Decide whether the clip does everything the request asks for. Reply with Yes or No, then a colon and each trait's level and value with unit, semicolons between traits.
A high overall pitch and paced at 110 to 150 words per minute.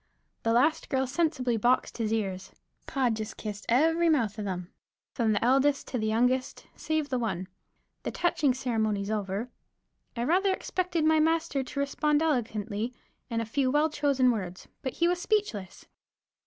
No: very high, 255 Hz; average, 165 wpm